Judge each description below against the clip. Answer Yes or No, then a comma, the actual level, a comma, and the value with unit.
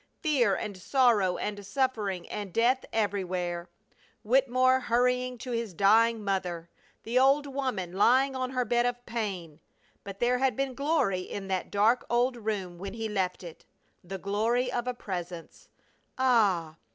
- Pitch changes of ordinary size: Yes, average, 4.7 semitones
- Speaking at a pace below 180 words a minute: Yes, average, 150 wpm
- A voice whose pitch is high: Yes, high, 225 Hz